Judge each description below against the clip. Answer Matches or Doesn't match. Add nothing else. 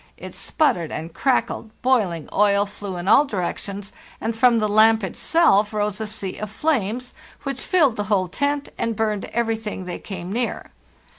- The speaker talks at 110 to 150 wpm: Doesn't match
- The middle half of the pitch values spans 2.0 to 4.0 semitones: Matches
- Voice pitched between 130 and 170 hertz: Doesn't match